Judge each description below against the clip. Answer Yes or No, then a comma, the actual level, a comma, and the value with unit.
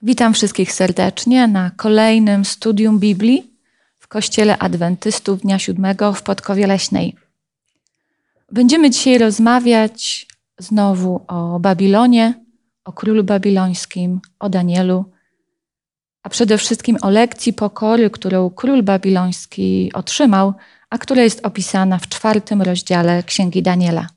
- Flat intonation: No, average, 3.5 semitones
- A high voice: Yes, high, 205 Hz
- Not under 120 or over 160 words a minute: No, slow, 110 wpm